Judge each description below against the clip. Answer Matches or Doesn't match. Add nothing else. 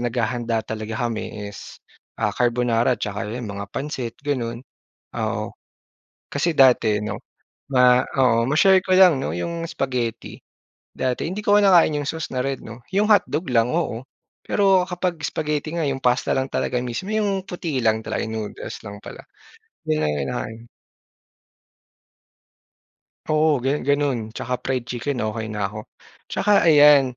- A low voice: Matches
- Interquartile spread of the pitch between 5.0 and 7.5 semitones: Matches